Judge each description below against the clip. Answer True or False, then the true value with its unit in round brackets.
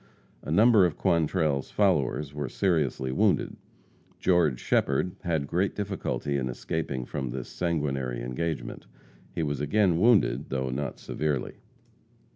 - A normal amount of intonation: True (4.8 semitones)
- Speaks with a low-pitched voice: True (75 Hz)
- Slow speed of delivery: True (125 wpm)